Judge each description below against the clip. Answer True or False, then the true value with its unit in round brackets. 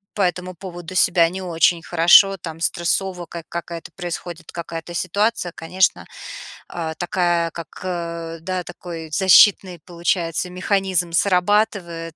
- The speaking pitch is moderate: True (175 Hz)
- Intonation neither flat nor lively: False (1.8 semitones)